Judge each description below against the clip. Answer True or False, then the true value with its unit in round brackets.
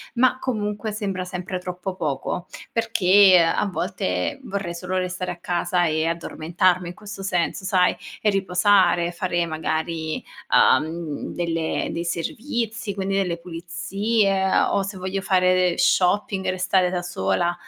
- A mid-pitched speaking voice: True (180 Hz)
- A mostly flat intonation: True (2.3 semitones)